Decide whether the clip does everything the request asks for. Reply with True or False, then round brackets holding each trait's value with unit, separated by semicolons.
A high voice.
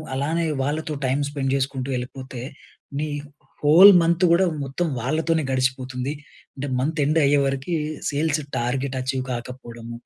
False (135 Hz)